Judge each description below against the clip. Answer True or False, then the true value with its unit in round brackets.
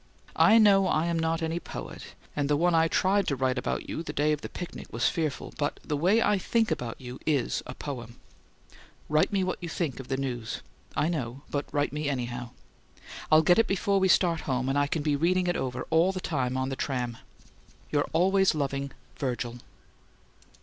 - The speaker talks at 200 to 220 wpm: True (205 wpm)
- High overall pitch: False (150 Hz)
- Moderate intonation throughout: True (5.0 semitones)